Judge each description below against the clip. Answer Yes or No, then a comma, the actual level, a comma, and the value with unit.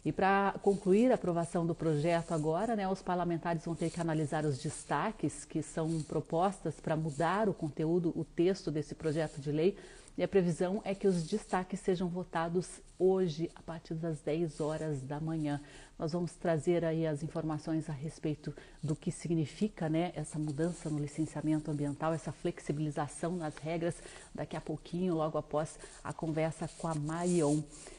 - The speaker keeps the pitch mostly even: Yes, narrow, 2.2 semitones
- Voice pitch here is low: No, medium, 165 Hz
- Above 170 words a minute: No, average, 165 wpm